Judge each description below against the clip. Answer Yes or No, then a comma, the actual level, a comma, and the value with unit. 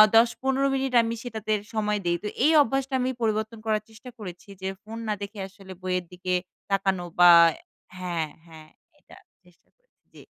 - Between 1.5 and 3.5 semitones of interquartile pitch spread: No, average, 3.9 semitones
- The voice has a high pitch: Yes, high, 210 Hz